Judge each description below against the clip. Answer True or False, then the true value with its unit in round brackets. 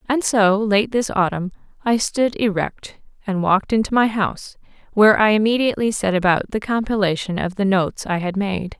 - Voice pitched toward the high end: True (205 Hz)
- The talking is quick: False (175 wpm)